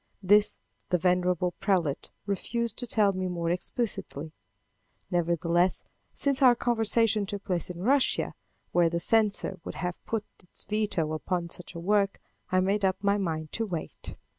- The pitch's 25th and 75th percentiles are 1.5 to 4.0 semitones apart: Yes, average, 3.3 semitones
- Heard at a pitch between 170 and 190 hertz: Yes, medium, 185 Hz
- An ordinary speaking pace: Yes, average, 155 wpm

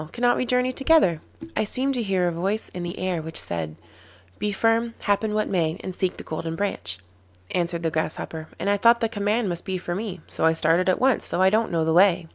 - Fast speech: Yes, fast, 235 wpm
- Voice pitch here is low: No, high, 190 Hz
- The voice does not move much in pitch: No, average, 4.8 semitones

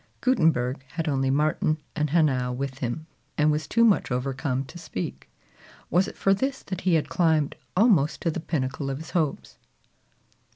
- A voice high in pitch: No, medium, 155 Hz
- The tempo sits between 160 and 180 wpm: Yes, average, 170 wpm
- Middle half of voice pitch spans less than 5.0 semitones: Yes, average, 4.0 semitones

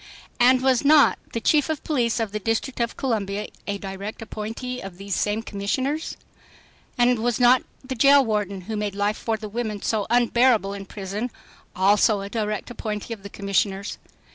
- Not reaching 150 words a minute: No, average, 175 wpm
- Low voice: No, high, 220 Hz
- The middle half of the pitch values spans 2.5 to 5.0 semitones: Yes, average, 3.3 semitones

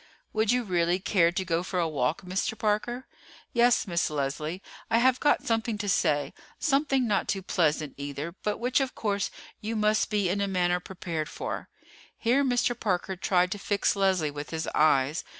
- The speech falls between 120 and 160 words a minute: No, average, 185 wpm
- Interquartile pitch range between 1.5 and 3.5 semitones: No, average, 5.0 semitones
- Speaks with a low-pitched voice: No, high, 195 Hz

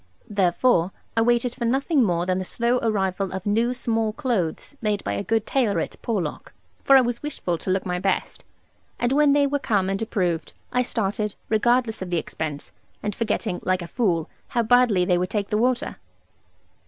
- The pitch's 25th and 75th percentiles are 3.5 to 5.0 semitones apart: Yes, average, 4.6 semitones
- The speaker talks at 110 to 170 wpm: No, average, 190 wpm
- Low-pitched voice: No, high, 215 Hz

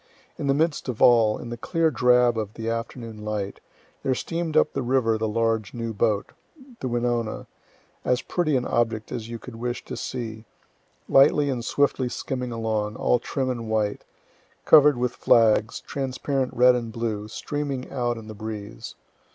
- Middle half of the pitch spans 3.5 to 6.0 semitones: No, average, 2.7 semitones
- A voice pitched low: Yes, low, 120 Hz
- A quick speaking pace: No, average, 170 wpm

